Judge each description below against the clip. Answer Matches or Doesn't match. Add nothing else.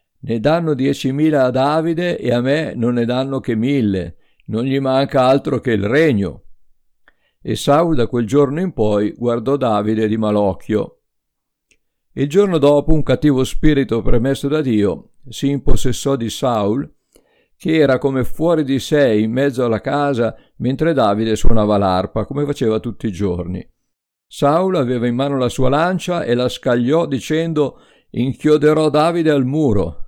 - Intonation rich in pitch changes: Doesn't match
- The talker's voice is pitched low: Matches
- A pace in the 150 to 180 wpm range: Matches